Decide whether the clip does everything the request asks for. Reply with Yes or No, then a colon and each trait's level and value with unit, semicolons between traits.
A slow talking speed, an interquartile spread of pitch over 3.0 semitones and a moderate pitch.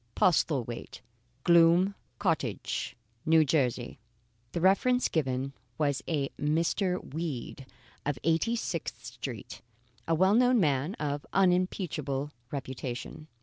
Yes: slow, 105 wpm; average, 4.7 semitones; medium, 160 Hz